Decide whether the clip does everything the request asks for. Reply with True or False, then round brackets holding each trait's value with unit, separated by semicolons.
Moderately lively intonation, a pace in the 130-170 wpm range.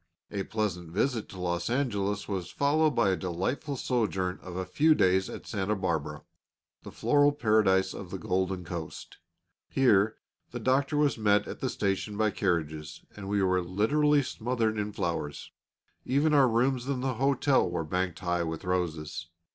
False (5.8 semitones; 165 wpm)